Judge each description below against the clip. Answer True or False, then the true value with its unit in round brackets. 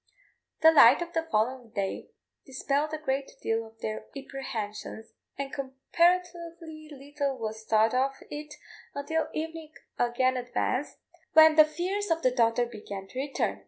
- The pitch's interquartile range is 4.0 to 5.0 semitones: True (4.7 semitones)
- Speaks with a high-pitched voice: True (275 Hz)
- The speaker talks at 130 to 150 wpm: True (145 wpm)